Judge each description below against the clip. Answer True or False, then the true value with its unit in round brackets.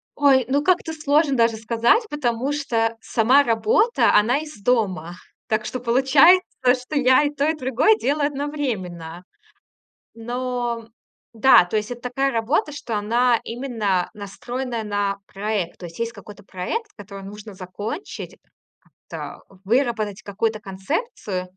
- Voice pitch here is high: True (235 Hz)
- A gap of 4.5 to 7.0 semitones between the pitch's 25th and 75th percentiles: True (4.8 semitones)